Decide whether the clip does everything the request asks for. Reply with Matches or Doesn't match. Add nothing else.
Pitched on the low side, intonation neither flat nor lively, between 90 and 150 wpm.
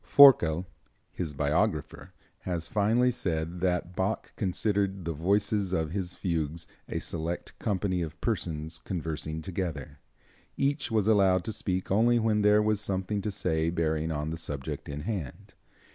Matches